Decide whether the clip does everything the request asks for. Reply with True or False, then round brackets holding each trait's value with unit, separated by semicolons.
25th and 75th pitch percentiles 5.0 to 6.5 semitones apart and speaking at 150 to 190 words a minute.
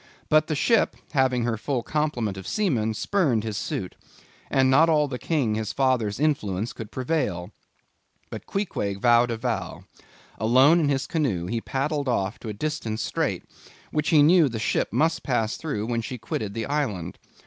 True (5.6 semitones; 175 wpm)